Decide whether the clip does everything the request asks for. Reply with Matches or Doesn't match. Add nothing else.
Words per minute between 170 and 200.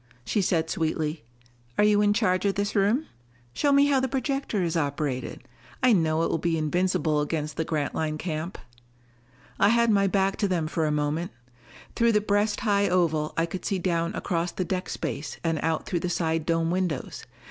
Matches